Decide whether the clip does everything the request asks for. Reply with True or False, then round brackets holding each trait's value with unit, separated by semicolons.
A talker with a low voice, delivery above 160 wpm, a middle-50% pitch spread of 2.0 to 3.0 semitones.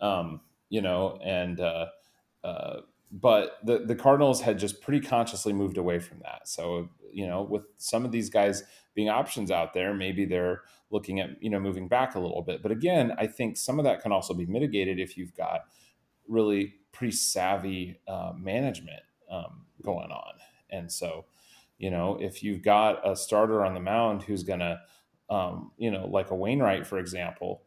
True (100 Hz; 185 wpm; 2.7 semitones)